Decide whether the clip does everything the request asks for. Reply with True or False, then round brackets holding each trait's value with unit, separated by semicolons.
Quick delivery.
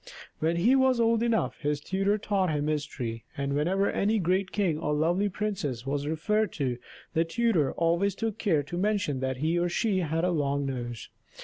False (190 wpm)